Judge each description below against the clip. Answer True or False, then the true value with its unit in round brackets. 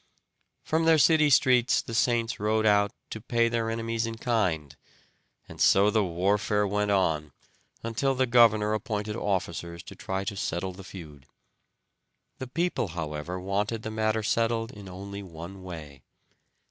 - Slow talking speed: False (150 wpm)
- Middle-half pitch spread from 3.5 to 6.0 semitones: True (3.8 semitones)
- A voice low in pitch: True (105 Hz)